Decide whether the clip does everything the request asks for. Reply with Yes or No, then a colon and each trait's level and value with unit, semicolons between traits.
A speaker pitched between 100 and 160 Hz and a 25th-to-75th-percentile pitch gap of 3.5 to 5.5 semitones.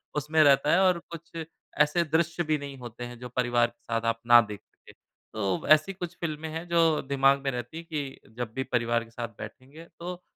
Yes: medium, 140 Hz; average, 5.2 semitones